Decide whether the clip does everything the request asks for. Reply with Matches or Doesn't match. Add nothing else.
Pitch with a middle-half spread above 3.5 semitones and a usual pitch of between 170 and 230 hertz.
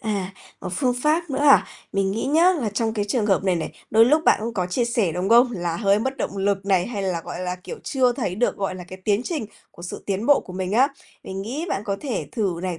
Matches